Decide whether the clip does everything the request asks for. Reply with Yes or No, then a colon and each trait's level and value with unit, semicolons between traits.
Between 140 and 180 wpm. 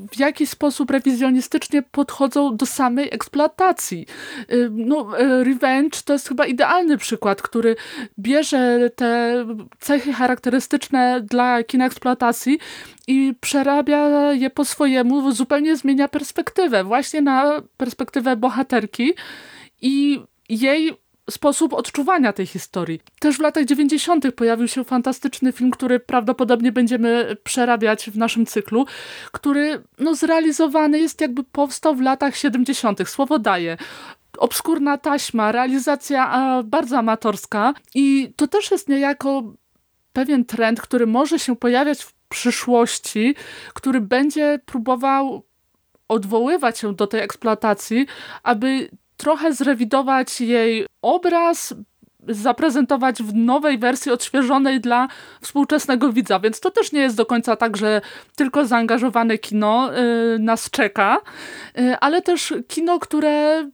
No: average, 115 wpm